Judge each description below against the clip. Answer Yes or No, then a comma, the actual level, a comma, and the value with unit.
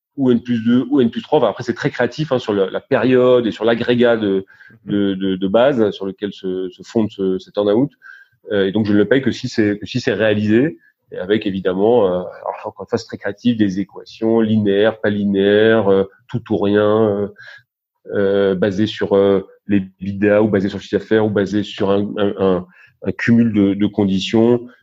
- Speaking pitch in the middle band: No, low, 105 Hz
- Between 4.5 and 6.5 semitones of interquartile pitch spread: No, average, 2.7 semitones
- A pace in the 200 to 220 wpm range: Yes, average, 215 wpm